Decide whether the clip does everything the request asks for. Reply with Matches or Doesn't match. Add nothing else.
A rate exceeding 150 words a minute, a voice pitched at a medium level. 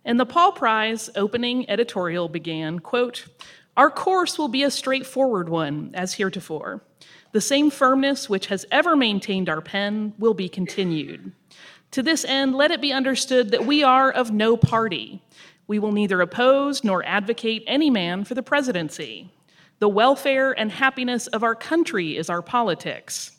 Doesn't match